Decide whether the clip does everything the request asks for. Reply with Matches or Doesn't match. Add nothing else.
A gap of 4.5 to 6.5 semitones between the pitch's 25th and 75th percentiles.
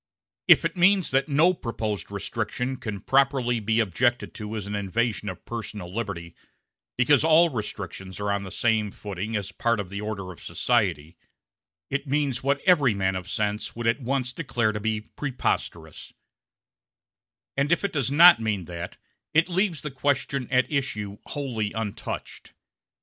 Matches